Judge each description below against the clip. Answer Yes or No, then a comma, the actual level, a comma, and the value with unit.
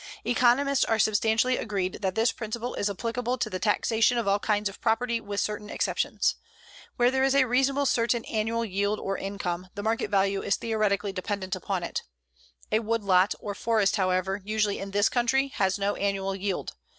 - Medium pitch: No, high, 210 Hz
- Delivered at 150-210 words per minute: Yes, average, 180 wpm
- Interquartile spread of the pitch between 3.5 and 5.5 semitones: No, average, 2.9 semitones